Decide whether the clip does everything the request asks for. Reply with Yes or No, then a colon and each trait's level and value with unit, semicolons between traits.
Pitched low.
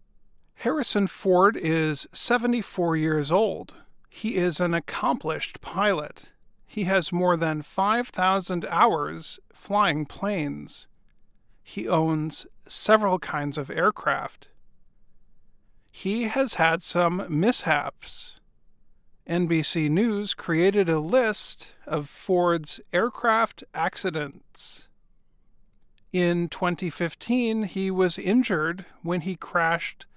No: medium, 180 Hz